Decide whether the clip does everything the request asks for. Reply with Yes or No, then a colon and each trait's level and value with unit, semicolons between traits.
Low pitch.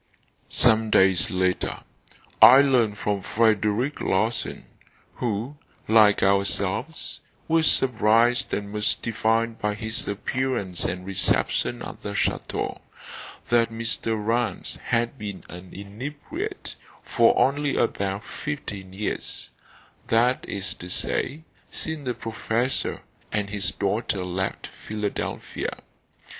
Yes: low, 110 Hz